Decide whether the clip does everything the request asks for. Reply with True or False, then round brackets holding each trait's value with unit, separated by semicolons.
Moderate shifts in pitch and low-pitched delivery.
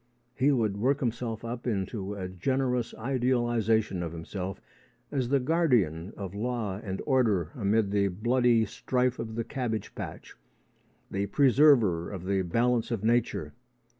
True (4.1 semitones; 115 Hz)